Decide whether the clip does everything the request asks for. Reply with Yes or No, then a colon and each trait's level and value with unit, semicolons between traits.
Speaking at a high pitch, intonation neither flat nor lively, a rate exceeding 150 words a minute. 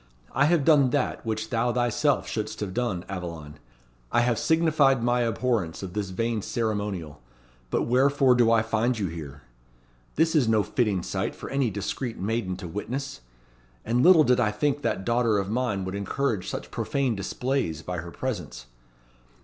No: low, 115 Hz; average, 4.9 semitones; average, 170 wpm